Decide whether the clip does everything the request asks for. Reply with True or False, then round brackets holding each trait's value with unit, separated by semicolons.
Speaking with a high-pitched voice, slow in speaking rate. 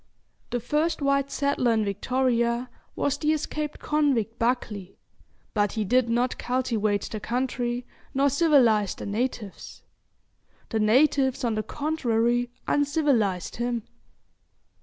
True (245 Hz; 115 wpm)